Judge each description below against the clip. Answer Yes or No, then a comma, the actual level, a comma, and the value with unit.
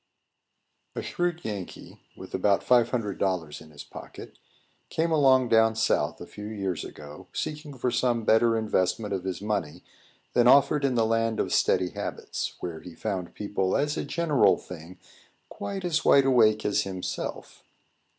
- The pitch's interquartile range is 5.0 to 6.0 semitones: Yes, wide, 5.6 semitones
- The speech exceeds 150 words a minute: Yes, average, 160 wpm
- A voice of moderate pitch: No, low, 110 Hz